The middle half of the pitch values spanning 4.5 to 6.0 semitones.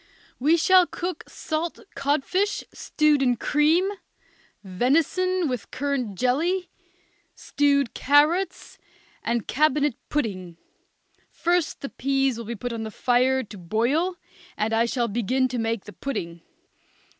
Yes: average, 5.0 semitones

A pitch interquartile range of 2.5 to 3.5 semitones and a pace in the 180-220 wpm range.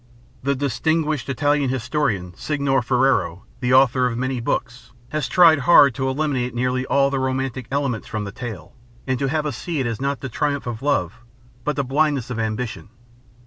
Yes: average, 2.8 semitones; average, 185 wpm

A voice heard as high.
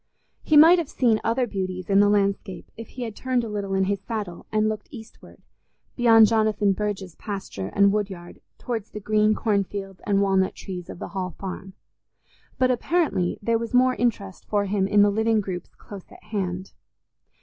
Yes: high, 205 Hz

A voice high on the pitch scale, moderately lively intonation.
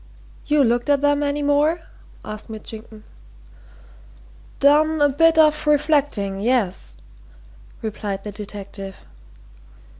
No: very high, 275 Hz; wide, 5.7 semitones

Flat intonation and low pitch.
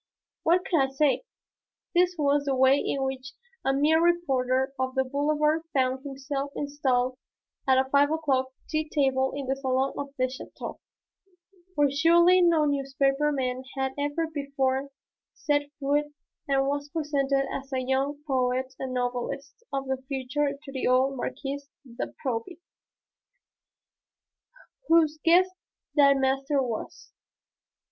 No: narrow, 1.9 semitones; very high, 275 Hz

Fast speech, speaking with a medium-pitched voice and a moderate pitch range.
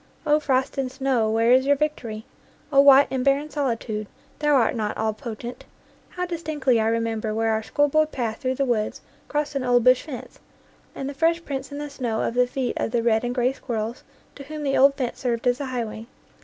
No: fast, 215 wpm; very high, 255 Hz; average, 3.6 semitones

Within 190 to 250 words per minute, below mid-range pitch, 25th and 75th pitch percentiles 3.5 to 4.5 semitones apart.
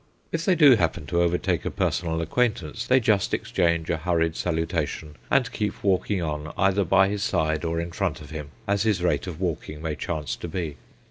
Yes: average, 200 wpm; very low, 85 Hz; average, 4.0 semitones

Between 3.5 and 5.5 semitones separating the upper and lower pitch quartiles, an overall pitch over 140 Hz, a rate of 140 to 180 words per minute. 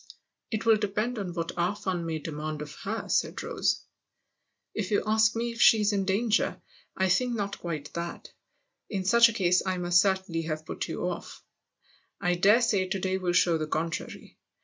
No: average, 3.9 semitones; high, 190 Hz; average, 200 wpm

